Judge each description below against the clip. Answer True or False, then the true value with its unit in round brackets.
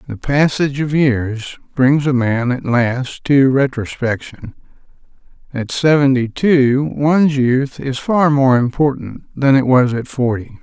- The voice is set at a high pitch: False (130 Hz)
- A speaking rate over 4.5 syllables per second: False (3.9 syllables/s)